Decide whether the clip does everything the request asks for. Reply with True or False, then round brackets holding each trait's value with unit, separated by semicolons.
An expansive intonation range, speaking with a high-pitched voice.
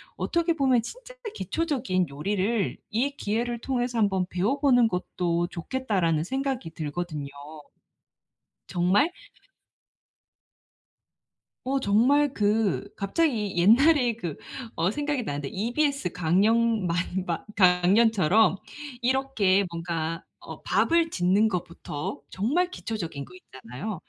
True (6.7 semitones; 210 Hz)